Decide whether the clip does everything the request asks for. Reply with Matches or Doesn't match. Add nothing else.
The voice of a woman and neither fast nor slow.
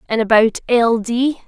Matches